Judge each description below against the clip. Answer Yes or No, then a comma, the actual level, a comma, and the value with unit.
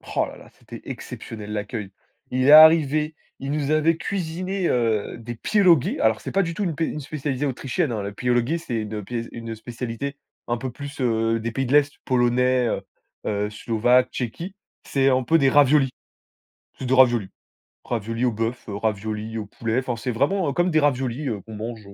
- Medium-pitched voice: No, low, 125 Hz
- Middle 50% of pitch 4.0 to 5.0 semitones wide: Yes, average, 4.5 semitones